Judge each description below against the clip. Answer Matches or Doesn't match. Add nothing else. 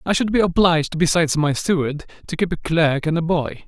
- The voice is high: Doesn't match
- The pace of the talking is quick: Matches